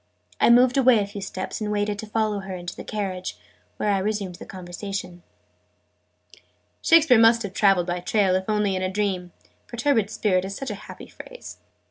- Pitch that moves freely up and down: No, average, 2.8 semitones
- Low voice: No, high, 205 Hz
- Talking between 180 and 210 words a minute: Yes, average, 185 wpm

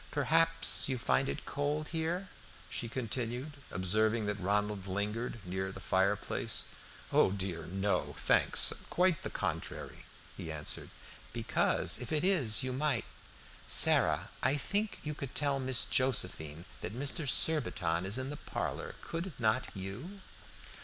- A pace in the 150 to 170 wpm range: No, average, 140 wpm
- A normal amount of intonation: No, wide, 7.0 semitones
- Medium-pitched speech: No, low, 125 Hz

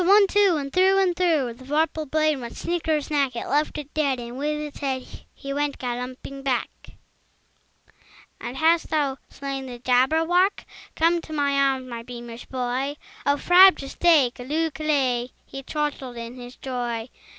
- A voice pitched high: Yes, very high, 280 Hz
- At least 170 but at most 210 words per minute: No, average, 160 wpm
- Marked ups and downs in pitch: No, average, 3.7 semitones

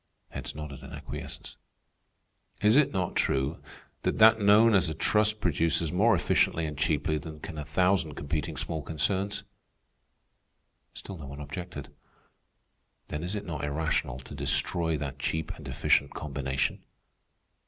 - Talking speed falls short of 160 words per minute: Yes, average, 145 wpm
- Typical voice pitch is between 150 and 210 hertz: No, very low, 80 Hz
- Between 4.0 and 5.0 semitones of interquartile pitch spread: Yes, average, 4.3 semitones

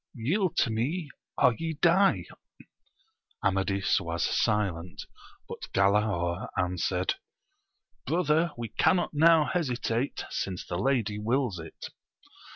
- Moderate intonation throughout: No, wide, 8.3 semitones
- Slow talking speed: Yes, slow, 105 wpm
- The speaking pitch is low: Yes, low, 115 Hz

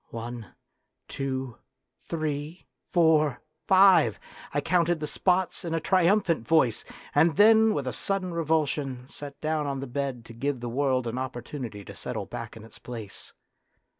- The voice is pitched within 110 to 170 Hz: Yes, medium, 140 Hz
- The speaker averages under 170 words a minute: Yes, average, 155 wpm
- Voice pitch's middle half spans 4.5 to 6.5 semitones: Yes, average, 5.2 semitones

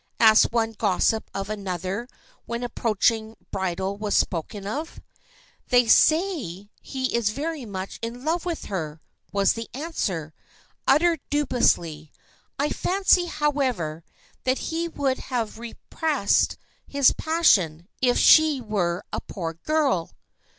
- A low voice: No, high, 230 Hz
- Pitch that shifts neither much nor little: No, wide, 7.1 semitones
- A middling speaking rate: No, slow, 125 wpm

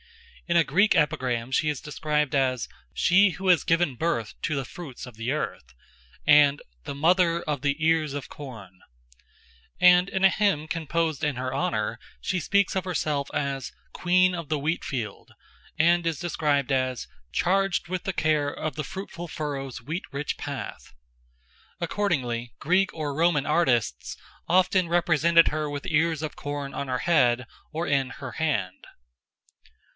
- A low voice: No, medium, 150 Hz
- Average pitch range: Yes, average, 4.0 semitones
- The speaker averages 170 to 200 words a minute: No, average, 160 wpm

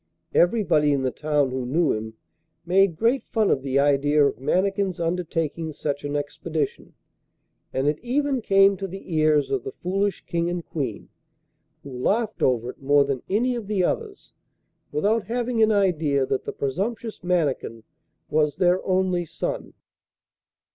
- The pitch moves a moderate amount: No, wide, 5.8 semitones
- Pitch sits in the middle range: Yes, medium, 170 Hz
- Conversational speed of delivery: Yes, average, 155 wpm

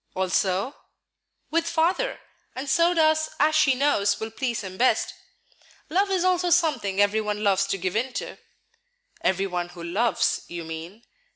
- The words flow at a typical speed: Yes, average, 160 wpm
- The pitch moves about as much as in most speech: No, wide, 8.6 semitones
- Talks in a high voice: Yes, high, 225 Hz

